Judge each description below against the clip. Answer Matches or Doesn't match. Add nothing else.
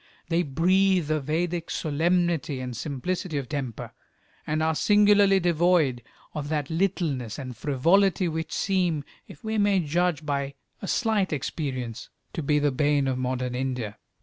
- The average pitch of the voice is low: Doesn't match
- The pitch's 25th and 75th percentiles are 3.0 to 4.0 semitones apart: Doesn't match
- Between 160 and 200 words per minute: Doesn't match